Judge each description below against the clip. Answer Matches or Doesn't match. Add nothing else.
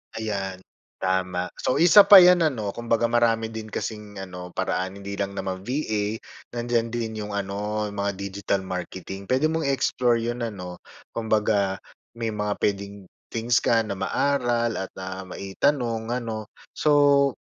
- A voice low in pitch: Matches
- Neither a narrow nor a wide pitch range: Matches